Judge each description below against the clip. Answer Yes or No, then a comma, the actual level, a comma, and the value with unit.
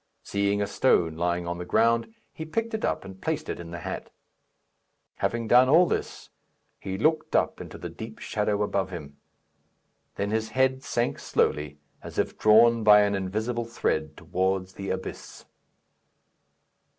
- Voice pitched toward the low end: Yes, low, 105 Hz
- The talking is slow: No, average, 160 wpm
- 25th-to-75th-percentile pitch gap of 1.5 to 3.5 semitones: No, average, 4.2 semitones